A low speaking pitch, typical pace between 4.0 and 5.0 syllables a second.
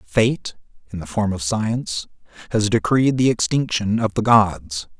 Yes: low, 110 Hz; 4.2 syllables/s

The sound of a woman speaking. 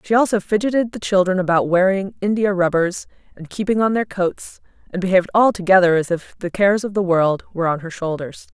Yes: female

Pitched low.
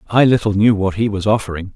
Yes: low, 105 Hz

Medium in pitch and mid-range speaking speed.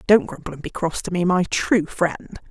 No: medium, 180 Hz; fast, 240 wpm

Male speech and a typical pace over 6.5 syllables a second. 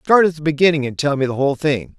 Yes: male; 6.7 syllables/s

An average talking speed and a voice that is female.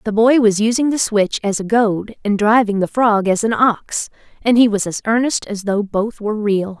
No: fast, 230 wpm; female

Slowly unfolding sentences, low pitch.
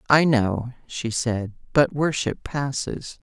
Yes: slow, 125 wpm; low, 130 Hz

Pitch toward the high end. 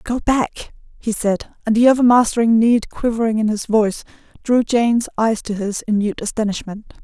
Yes: high, 225 Hz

